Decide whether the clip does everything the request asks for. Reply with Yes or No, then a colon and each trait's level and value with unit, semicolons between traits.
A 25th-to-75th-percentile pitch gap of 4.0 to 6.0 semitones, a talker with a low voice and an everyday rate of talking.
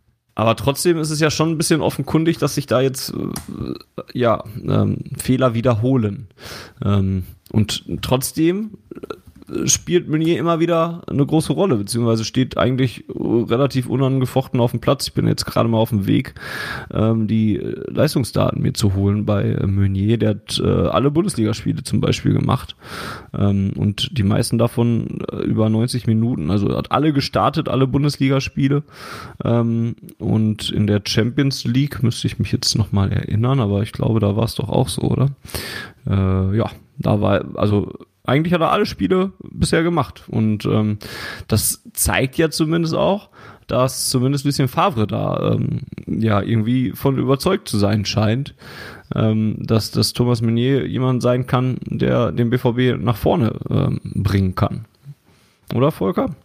Yes: average, 4.6 semitones; low, 120 Hz; average, 150 wpm